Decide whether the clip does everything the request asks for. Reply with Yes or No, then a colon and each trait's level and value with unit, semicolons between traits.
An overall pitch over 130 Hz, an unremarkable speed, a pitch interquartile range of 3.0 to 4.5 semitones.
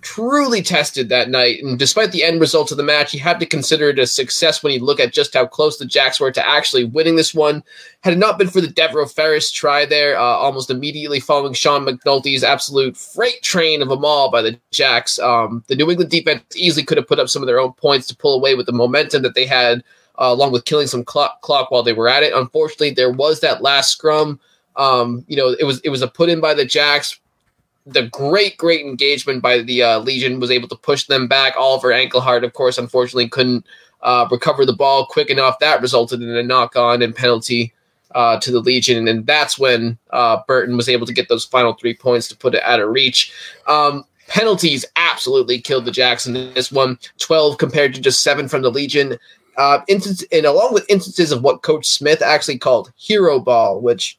No: medium, 140 Hz; fast, 225 wpm; average, 4.1 semitones